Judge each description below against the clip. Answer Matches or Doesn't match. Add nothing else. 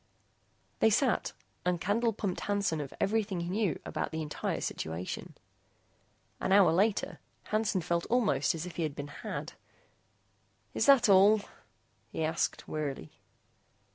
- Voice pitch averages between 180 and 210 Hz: Matches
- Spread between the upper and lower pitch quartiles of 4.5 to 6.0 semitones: Matches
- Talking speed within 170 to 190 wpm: Doesn't match